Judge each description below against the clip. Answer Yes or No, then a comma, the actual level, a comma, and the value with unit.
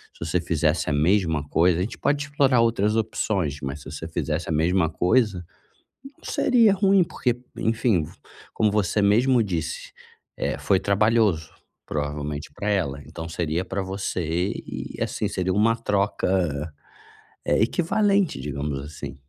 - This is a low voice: Yes, very low, 95 Hz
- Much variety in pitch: Yes, wide, 5.9 semitones